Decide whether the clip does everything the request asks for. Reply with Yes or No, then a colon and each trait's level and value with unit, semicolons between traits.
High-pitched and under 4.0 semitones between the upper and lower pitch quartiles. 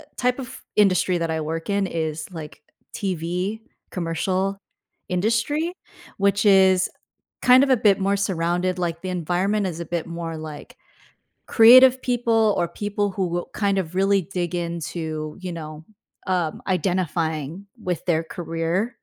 No: medium, 180 Hz; average, 3.3 semitones